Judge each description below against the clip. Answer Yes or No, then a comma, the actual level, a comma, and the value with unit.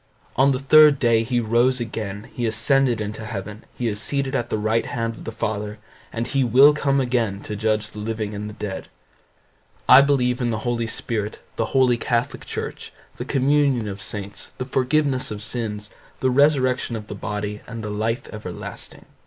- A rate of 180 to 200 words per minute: Yes, average, 185 wpm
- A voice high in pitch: No, low, 115 Hz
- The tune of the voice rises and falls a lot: No, average, 3.4 semitones